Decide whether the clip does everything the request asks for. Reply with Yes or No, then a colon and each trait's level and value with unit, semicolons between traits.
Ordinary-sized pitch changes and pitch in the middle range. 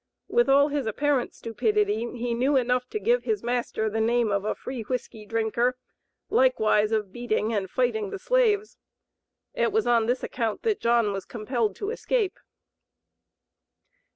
No: average, 4.6 semitones; high, 240 Hz